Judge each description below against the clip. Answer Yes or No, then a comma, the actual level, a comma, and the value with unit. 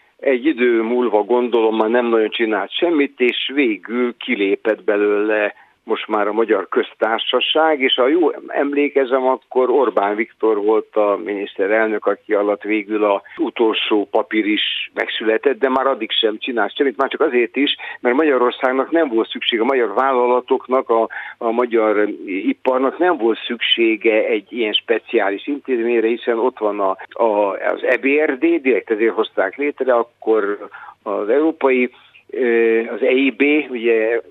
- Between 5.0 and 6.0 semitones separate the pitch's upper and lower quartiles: Yes, wide, 5.6 semitones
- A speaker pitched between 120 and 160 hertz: Yes, low, 130 Hz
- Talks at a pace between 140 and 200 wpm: Yes, average, 145 wpm